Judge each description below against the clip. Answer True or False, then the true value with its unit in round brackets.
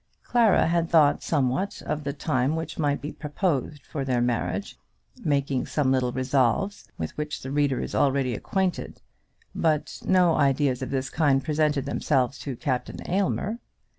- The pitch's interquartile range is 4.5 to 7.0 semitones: False (3.4 semitones)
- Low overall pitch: False (145 Hz)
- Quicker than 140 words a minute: True (155 wpm)